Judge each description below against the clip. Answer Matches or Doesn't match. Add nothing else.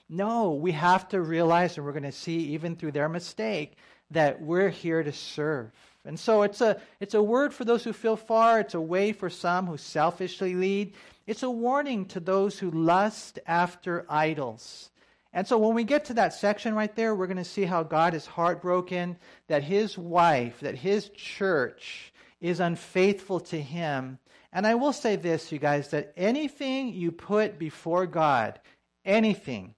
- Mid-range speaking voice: Matches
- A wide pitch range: Doesn't match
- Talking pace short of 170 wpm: Doesn't match